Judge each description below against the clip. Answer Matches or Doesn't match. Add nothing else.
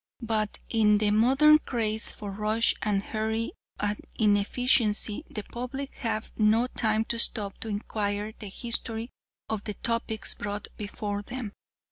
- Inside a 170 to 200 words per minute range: Doesn't match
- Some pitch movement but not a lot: Doesn't match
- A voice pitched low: Doesn't match